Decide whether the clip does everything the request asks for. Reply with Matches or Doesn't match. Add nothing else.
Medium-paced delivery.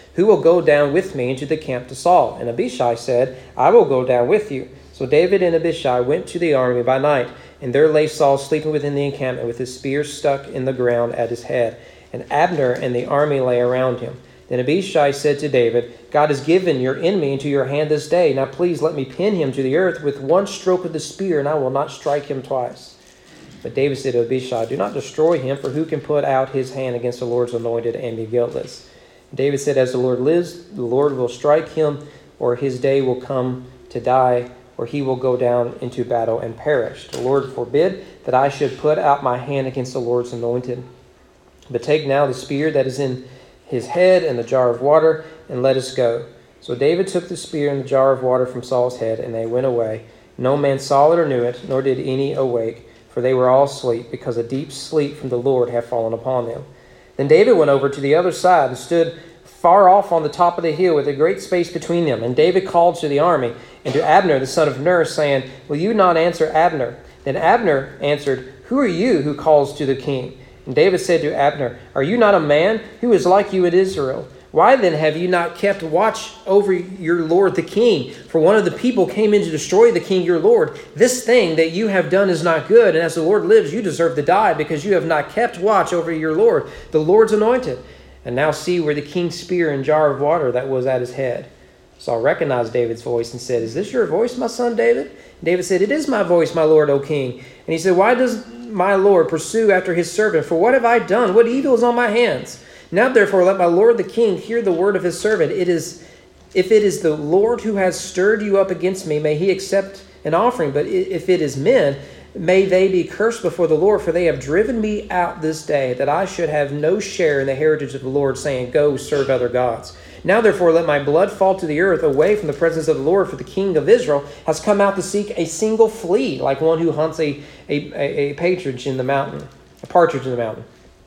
Doesn't match